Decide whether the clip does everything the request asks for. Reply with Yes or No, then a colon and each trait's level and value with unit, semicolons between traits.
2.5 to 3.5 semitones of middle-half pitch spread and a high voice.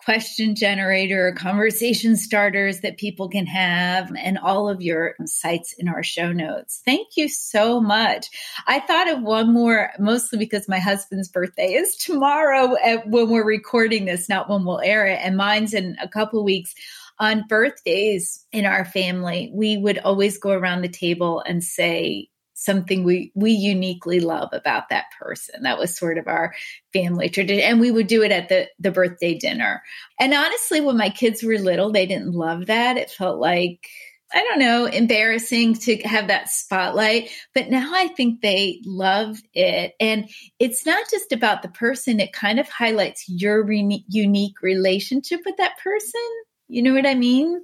No: average, 3.9 semitones; high, 210 Hz